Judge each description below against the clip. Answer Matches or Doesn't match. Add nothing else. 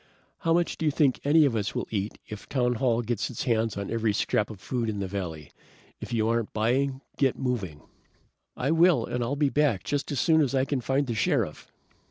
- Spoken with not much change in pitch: Doesn't match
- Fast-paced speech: Matches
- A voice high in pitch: Doesn't match